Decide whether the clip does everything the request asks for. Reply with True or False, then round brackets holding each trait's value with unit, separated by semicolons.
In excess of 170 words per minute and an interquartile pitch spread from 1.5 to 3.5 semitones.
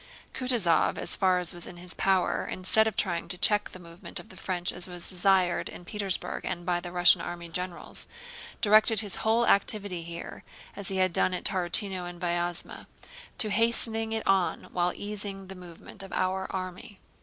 True (185 wpm; 2.5 semitones)